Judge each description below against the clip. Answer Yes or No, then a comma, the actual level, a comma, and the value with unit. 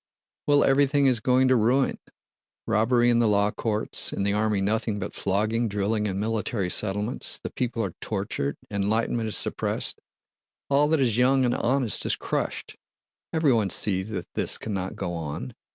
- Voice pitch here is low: Yes, low, 110 Hz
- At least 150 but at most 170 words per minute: Yes, average, 165 wpm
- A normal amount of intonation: Yes, average, 3.7 semitones